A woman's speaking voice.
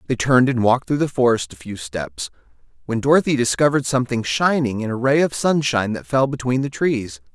No: male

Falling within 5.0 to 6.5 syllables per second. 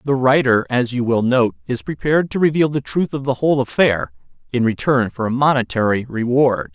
Yes: 5.5 syllables/s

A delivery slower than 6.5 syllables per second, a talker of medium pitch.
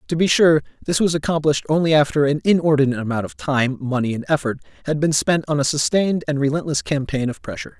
No: 6.6 syllables/s; medium, 150 Hz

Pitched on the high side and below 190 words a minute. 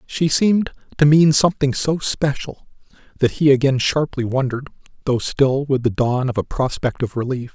No: low, 135 Hz; average, 175 wpm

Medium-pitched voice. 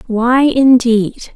No: high, 245 Hz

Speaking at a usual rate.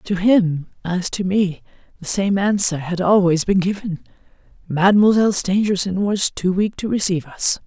Yes: average, 155 wpm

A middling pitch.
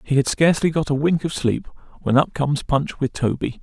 Yes: medium, 145 Hz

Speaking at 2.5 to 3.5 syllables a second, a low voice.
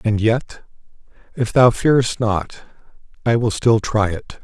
Yes: 3.3 syllables/s; low, 115 Hz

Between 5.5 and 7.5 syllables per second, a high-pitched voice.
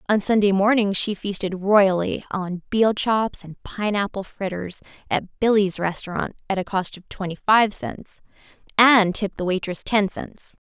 No: 4.4 syllables/s; high, 200 Hz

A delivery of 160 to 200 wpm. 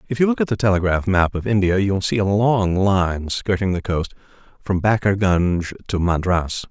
Yes: average, 195 wpm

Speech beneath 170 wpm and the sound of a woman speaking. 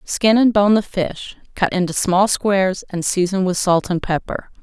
No: average, 195 wpm; female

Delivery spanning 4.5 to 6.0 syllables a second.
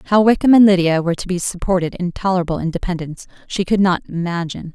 No: 6.8 syllables/s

